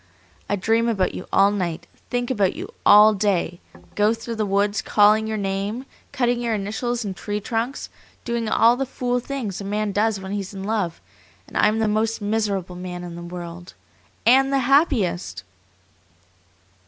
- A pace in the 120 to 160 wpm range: No, average, 175 wpm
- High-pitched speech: Yes, high, 210 Hz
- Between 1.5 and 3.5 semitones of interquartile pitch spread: Yes, average, 3.1 semitones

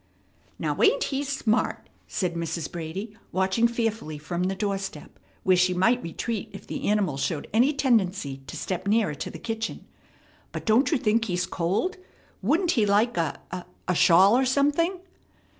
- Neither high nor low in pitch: No, high, 205 Hz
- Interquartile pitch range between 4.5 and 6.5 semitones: Yes, average, 5.0 semitones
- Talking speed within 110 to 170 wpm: Yes, average, 165 wpm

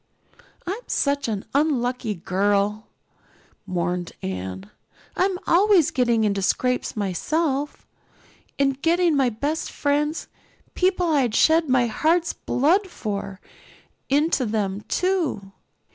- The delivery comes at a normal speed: No, slow, 105 wpm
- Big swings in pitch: Yes, wide, 7.7 semitones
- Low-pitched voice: No, very high, 265 Hz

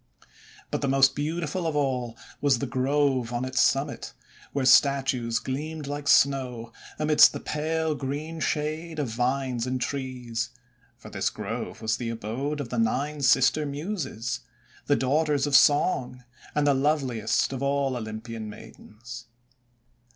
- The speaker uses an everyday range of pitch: Yes, average, 3.1 semitones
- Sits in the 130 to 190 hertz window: Yes, low, 135 Hz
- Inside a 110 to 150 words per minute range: Yes, average, 145 wpm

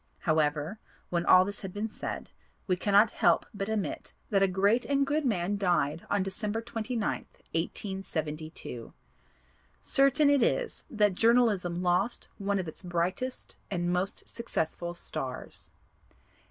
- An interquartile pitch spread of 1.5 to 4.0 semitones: No, average, 4.4 semitones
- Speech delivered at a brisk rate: No, slow, 135 wpm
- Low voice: No, high, 195 Hz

